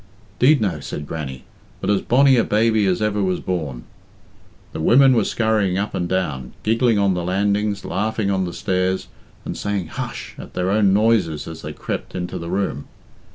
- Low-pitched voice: Yes, very low, 95 Hz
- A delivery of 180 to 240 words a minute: Yes, average, 185 wpm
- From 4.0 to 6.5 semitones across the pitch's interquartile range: No, average, 3.4 semitones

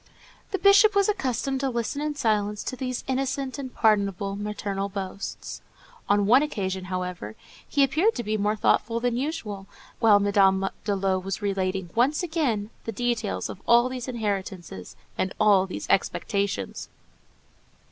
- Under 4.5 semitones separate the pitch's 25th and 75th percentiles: No, average, 4.8 semitones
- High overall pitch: Yes, high, 215 Hz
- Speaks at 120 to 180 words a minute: Yes, average, 150 wpm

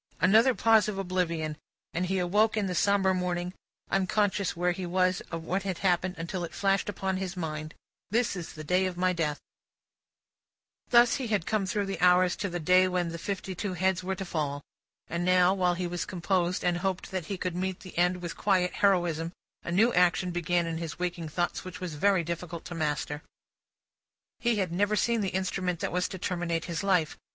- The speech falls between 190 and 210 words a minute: Yes, fast, 205 wpm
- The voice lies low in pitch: No, medium, 180 Hz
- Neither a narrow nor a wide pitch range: No, narrow, 2.0 semitones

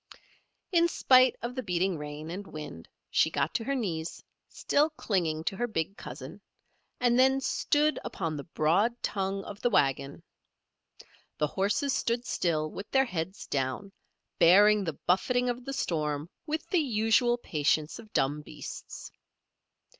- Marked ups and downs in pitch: Yes, wide, 7.6 semitones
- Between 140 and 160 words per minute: Yes, average, 150 wpm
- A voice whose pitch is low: No, high, 195 Hz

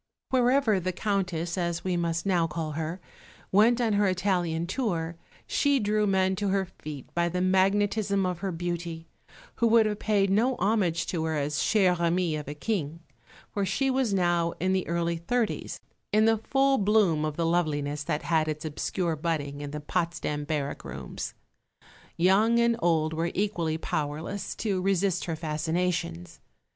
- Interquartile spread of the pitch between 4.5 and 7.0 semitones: No, average, 3.8 semitones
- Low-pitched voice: No, medium, 175 Hz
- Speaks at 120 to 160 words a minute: No, average, 170 wpm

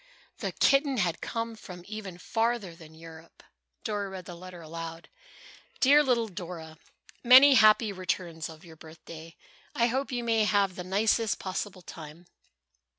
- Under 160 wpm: Yes, average, 150 wpm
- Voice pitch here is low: No, medium, 185 Hz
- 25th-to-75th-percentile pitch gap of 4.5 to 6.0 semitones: Yes, average, 5.3 semitones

